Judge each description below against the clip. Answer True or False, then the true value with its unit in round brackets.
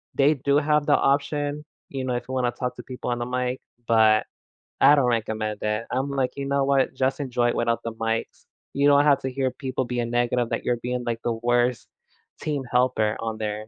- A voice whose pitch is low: True (125 Hz)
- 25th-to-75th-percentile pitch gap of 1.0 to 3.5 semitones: True (2.9 semitones)